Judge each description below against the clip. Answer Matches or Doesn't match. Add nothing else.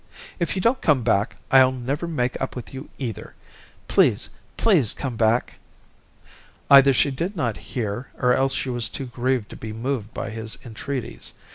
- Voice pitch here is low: Matches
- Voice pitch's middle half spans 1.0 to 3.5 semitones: Matches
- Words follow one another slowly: Doesn't match